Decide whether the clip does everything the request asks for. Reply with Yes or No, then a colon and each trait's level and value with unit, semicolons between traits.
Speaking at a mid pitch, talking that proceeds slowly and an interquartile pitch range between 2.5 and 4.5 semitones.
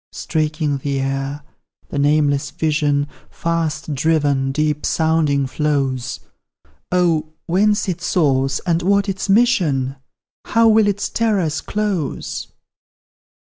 Yes: medium, 155 Hz; slow, 105 wpm; average, 4.0 semitones